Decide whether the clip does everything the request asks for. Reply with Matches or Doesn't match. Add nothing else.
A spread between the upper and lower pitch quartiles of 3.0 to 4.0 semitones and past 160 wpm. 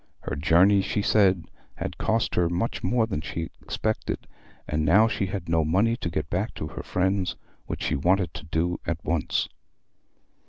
Matches